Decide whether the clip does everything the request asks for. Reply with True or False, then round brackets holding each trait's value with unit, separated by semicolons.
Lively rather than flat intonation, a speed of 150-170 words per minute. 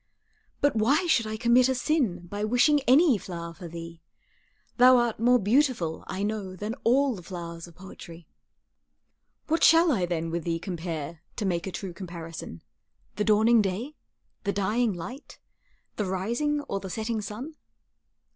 True (6.1 semitones; 160 wpm)